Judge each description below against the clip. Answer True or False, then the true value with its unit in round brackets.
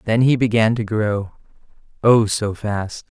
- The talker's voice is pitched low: True (110 Hz)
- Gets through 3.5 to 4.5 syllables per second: True (3.8 syllables/s)